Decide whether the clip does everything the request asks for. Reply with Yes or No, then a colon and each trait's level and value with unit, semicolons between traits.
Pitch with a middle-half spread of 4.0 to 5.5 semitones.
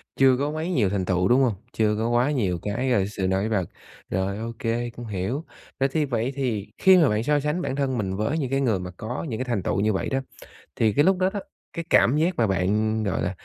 Yes: average, 5.1 semitones